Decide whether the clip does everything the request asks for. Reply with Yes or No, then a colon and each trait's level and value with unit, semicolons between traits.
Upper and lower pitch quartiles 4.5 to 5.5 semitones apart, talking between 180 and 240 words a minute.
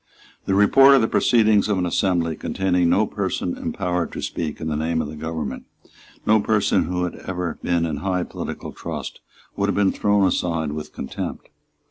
No: average, 3.6 semitones; average, 185 wpm